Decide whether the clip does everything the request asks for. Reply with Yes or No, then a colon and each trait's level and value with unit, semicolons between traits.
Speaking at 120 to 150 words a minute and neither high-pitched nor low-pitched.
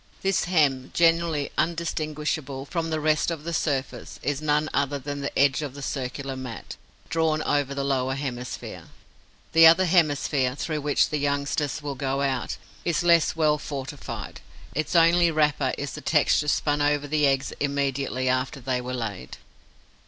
No: average, 160 wpm; medium, 145 Hz